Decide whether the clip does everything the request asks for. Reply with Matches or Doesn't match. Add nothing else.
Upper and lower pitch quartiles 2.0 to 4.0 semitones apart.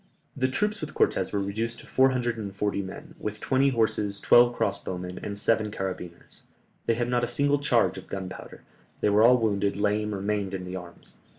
Matches